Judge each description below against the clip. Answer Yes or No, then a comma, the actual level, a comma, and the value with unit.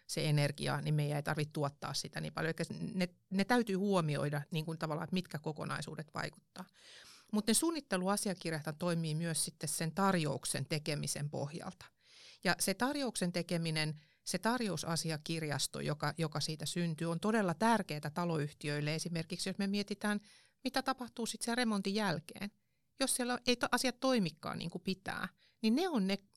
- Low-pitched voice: No, medium, 175 Hz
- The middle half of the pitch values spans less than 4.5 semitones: No, average, 5.0 semitones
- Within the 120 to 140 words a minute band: No, fast, 155 wpm